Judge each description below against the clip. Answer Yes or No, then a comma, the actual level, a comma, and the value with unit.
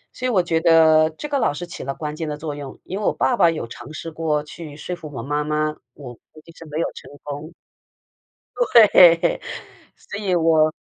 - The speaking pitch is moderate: Yes, medium, 155 Hz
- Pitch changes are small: Yes, narrow, 2.2 semitones